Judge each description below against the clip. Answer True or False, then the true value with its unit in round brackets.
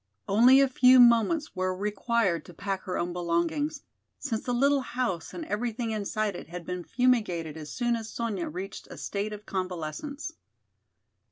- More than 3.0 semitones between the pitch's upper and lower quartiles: True (5.3 semitones)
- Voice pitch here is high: True (215 Hz)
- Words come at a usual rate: True (165 wpm)